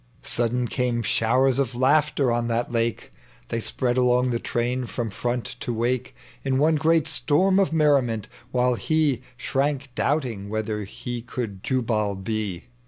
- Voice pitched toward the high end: No, low, 125 Hz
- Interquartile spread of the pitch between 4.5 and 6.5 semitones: No, average, 2.9 semitones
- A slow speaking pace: No, average, 150 wpm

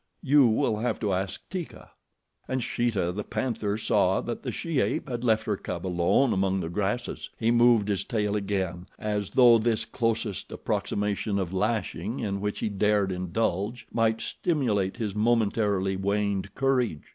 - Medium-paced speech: Yes, average, 160 wpm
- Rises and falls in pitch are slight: No, average, 3.3 semitones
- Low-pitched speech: Yes, low, 105 Hz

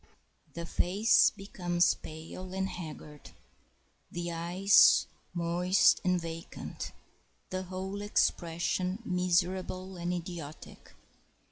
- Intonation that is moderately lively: No, narrow, 1.7 semitones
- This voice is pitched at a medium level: Yes, medium, 180 Hz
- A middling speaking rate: No, slow, 95 wpm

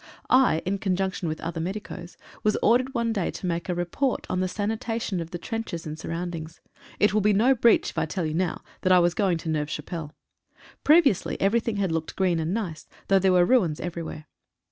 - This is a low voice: No, medium, 185 Hz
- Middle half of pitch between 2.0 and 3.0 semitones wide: No, average, 4.2 semitones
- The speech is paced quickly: Yes, fast, 210 wpm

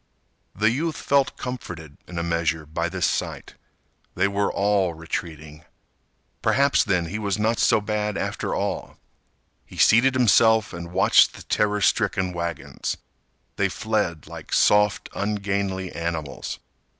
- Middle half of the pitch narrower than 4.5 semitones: Yes, average, 3.9 semitones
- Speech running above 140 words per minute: No, slow, 135 wpm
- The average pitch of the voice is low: Yes, low, 100 Hz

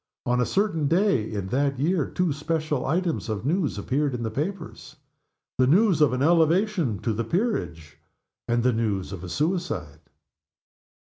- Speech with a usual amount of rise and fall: No, wide, 6.9 semitones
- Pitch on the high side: No, medium, 140 Hz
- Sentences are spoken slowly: No, average, 165 wpm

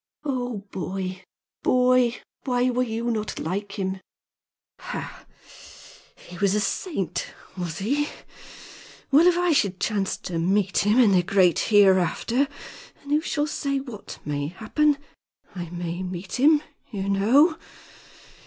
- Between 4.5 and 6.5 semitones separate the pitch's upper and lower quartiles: Yes, wide, 5.5 semitones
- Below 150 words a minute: Yes, slow, 135 wpm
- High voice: Yes, high, 210 Hz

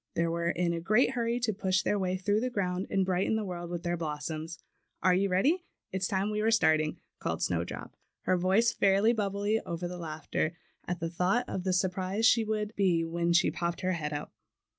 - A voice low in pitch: No, medium, 185 Hz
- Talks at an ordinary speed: No, fast, 220 wpm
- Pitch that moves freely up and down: No, average, 3.5 semitones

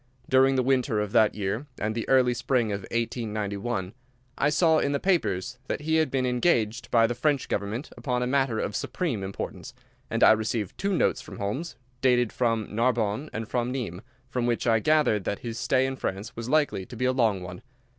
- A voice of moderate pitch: No, low, 120 Hz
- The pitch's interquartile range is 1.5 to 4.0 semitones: Yes, average, 3.6 semitones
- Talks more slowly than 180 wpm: No, fast, 205 wpm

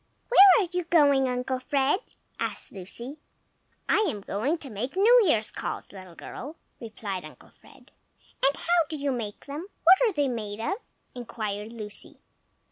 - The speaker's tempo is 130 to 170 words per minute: Yes, average, 160 wpm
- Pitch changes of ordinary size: No, wide, 7.4 semitones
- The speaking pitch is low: No, very high, 265 Hz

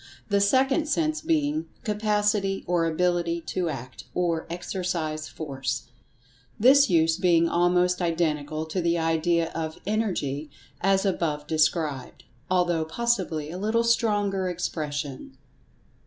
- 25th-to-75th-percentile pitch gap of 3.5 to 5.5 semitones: Yes, average, 4.3 semitones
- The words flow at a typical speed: No, slow, 115 wpm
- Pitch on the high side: No, medium, 175 Hz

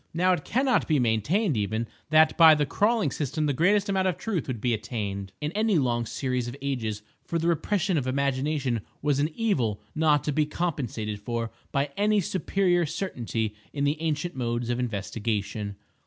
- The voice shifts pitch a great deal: Yes, wide, 6.5 semitones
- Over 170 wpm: Yes, average, 180 wpm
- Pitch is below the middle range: No, medium, 145 Hz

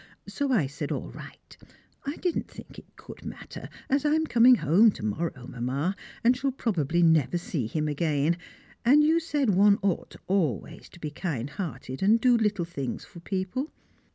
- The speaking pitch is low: No, medium, 180 Hz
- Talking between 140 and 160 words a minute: No, average, 180 wpm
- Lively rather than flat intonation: Yes, wide, 8.5 semitones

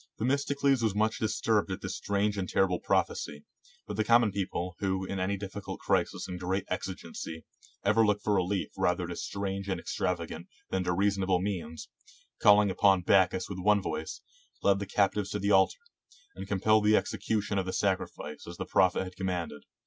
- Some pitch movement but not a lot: No, narrow, 2.0 semitones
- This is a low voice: Yes, very low, 95 Hz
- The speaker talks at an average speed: Yes, average, 185 wpm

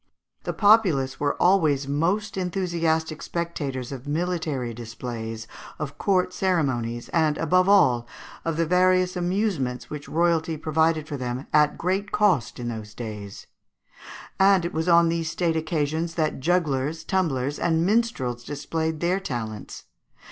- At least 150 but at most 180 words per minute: No, slow, 135 wpm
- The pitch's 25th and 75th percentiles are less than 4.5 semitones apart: No, average, 5.1 semitones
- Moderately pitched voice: Yes, medium, 160 Hz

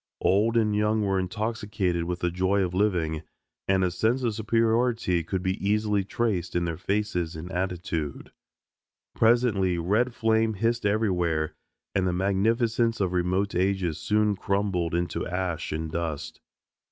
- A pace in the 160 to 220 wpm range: No, average, 145 wpm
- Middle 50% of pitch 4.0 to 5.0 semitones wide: No, average, 3.5 semitones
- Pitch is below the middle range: Yes, very low, 95 Hz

